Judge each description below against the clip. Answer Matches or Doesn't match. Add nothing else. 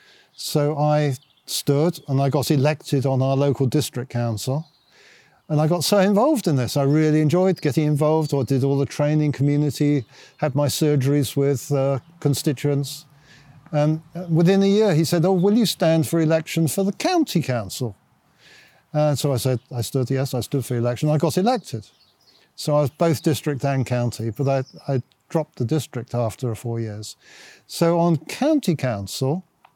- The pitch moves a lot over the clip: Doesn't match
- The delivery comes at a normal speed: Matches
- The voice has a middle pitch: Matches